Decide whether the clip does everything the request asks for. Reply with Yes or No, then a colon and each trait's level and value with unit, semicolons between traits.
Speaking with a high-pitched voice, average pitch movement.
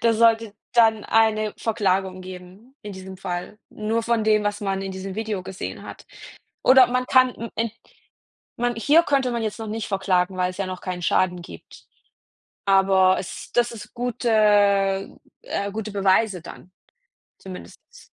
Yes: high, 205 Hz; average, 3.2 semitones